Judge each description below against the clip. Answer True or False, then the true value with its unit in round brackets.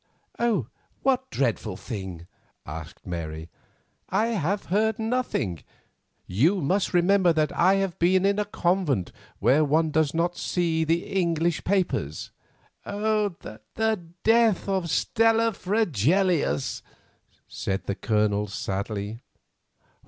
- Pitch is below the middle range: False (170 Hz)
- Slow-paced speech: True (110 wpm)